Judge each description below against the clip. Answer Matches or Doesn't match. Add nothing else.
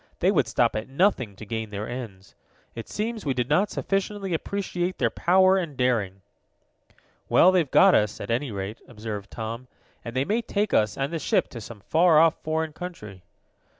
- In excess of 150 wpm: Matches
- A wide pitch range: Matches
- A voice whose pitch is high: Doesn't match